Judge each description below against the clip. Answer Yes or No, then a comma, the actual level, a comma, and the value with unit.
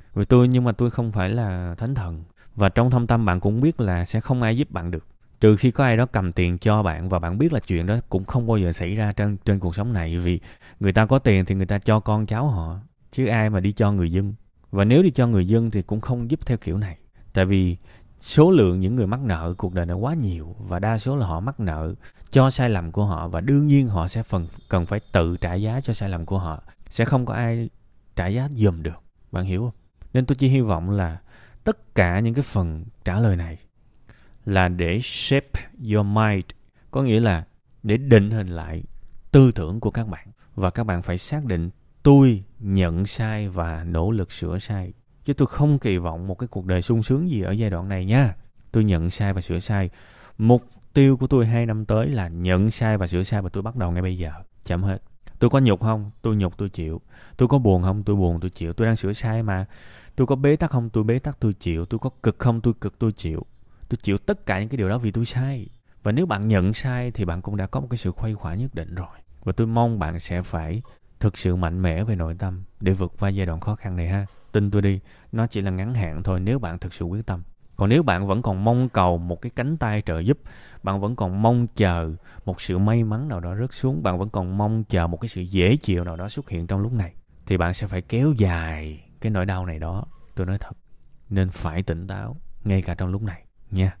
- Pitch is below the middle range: Yes, low, 100 Hz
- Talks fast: Yes, fast, 255 wpm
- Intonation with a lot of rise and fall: No, average, 4.3 semitones